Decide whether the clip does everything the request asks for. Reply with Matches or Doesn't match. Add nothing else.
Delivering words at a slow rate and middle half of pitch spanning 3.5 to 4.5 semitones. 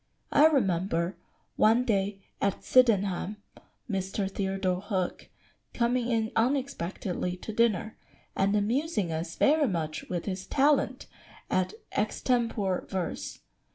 Matches